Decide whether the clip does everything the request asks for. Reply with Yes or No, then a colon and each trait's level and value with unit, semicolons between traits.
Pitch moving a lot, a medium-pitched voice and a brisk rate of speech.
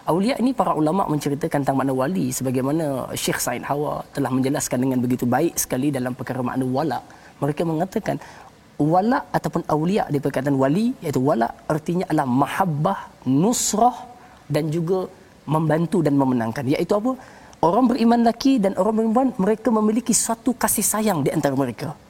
Yes: wide, 8.0 semitones; medium, 155 Hz; fast, 155 wpm